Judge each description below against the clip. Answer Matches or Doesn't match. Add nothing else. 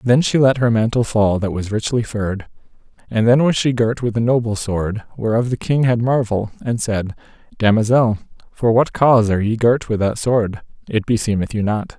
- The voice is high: Doesn't match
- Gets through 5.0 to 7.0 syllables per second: Matches